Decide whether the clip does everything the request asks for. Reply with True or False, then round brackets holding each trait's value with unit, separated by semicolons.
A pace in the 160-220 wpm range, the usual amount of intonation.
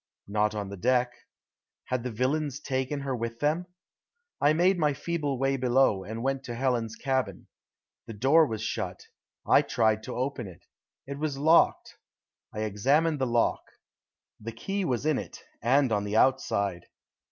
True (165 wpm; 4.4 semitones)